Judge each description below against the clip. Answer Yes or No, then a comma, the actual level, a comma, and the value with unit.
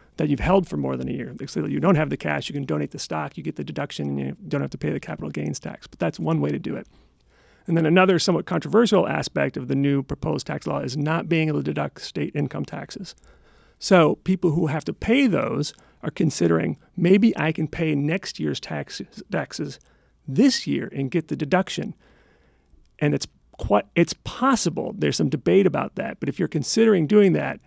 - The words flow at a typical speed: No, fast, 215 wpm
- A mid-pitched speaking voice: Yes, medium, 155 Hz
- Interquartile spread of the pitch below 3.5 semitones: No, wide, 5.4 semitones